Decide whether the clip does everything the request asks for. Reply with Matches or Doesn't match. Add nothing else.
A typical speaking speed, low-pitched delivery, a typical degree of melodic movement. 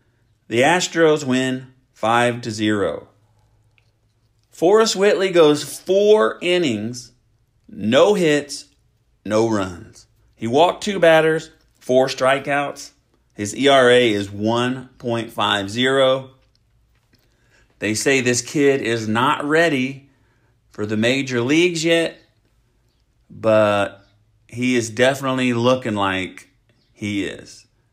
Doesn't match